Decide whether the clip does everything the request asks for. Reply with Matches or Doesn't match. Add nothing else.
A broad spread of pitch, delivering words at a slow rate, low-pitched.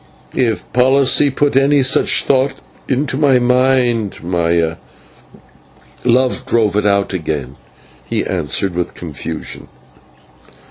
Matches